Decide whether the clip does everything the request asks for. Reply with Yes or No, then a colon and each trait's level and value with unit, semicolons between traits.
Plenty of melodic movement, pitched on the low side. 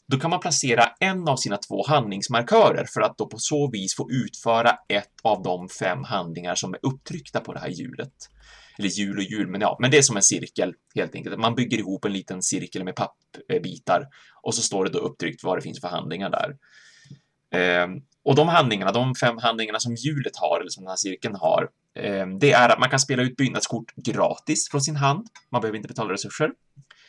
Yes: wide, 5.9 semitones; low, 120 Hz